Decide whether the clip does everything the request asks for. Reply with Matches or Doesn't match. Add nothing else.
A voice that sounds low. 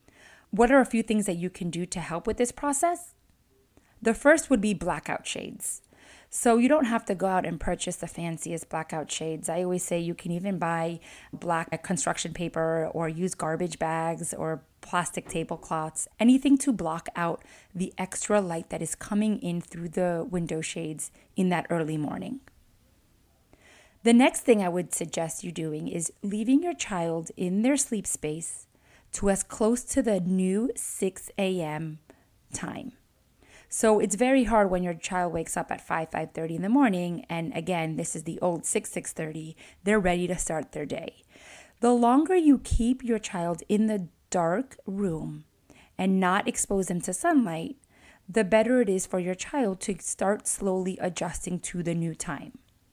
Doesn't match